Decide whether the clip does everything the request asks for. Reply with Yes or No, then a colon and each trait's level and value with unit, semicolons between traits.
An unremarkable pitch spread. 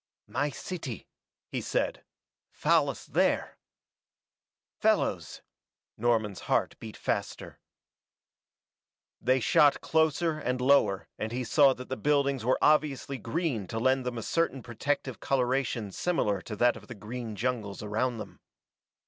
Yes: average, 3.8 semitones